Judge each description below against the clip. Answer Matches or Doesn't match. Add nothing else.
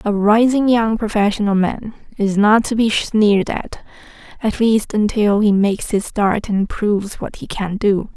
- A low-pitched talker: Doesn't match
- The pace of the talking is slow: Doesn't match